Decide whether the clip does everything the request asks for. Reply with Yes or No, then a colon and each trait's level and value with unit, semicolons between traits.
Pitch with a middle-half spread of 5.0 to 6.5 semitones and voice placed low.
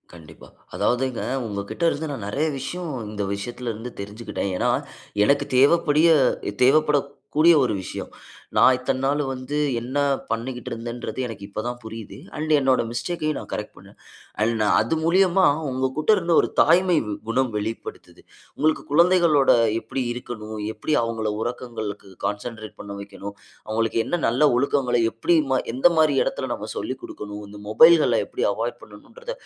Yes: wide, 5.5 semitones; low, 125 Hz